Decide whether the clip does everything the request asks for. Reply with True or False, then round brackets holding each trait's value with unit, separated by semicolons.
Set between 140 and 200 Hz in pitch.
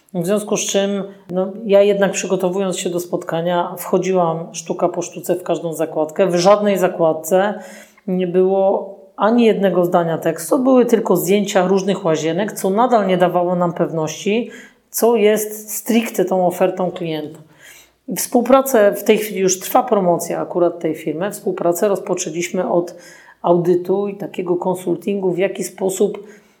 True (190 Hz)